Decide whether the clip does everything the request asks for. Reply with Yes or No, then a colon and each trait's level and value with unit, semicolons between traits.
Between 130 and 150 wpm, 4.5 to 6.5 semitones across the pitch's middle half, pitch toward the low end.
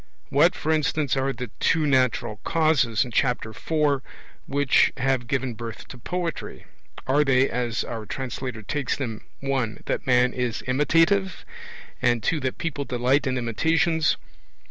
No: average, 145 wpm; average, 3.6 semitones; low, 130 Hz